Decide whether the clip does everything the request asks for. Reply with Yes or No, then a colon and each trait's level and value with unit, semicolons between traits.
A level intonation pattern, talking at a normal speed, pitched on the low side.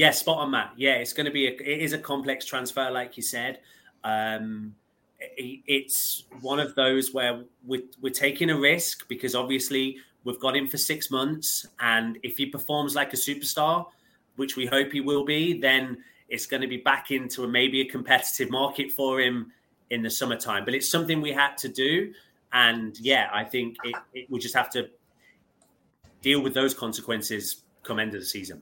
Yes: narrow, 2.0 semitones; average, 195 wpm; low, 130 Hz